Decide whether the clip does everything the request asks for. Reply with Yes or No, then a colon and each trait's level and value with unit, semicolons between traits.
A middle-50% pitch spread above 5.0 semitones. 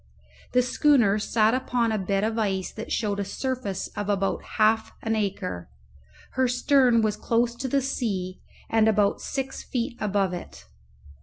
No: average, 3.6 semitones